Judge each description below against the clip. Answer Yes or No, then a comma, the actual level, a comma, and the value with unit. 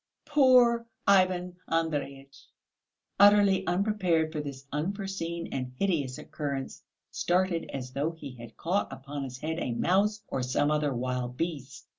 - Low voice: No, medium, 160 Hz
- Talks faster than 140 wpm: No, slow, 135 wpm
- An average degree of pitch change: No, wide, 5.8 semitones